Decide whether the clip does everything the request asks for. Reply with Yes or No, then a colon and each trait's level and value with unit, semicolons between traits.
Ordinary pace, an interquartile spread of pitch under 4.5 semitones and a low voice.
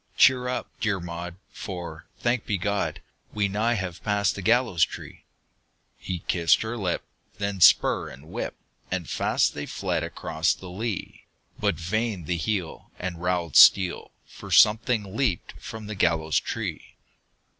Yes: average, 150 wpm; average, 4.1 semitones; very low, 95 Hz